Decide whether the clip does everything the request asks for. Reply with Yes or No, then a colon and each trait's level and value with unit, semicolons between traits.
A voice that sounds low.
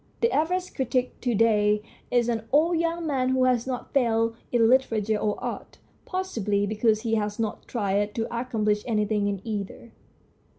No: high, 230 Hz